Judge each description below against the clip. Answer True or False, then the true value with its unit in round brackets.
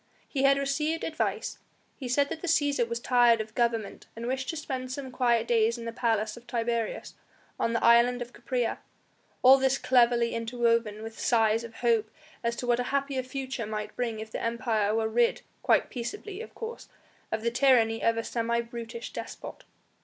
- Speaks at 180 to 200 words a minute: True (190 wpm)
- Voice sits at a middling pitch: False (235 Hz)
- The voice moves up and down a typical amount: False (2.3 semitones)